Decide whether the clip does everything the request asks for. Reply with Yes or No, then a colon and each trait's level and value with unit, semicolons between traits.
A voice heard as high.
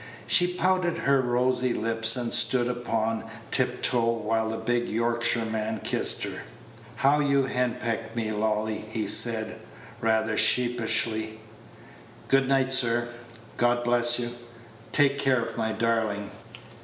No: low, 120 Hz